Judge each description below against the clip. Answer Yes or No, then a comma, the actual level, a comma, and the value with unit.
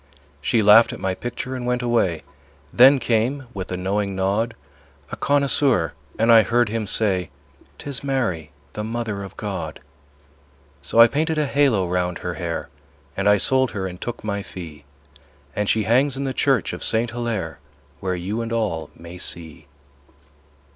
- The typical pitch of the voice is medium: No, low, 110 Hz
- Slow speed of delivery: No, average, 170 wpm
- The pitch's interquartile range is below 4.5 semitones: No, average, 4.8 semitones